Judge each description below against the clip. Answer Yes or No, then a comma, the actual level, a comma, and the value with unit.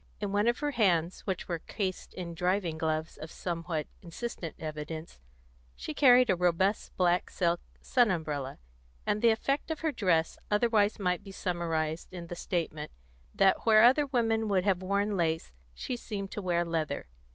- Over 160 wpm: Yes, average, 170 wpm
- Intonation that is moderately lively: Yes, average, 4.2 semitones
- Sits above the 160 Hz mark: Yes, medium, 185 Hz